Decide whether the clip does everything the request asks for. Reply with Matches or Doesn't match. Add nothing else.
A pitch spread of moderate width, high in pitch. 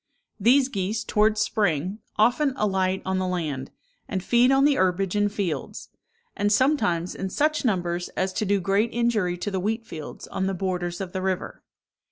Matches